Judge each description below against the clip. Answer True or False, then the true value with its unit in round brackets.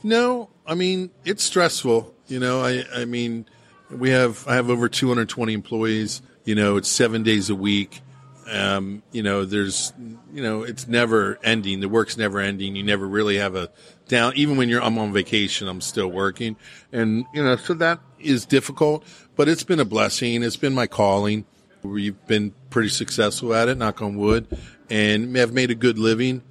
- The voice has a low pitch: True (115 Hz)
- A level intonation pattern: False (3.7 semitones)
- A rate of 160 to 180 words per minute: False (195 wpm)